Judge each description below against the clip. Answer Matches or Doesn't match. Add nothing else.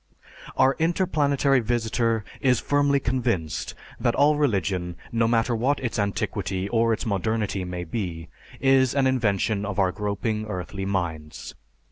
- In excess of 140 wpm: Doesn't match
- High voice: Doesn't match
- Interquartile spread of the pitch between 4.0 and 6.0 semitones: Matches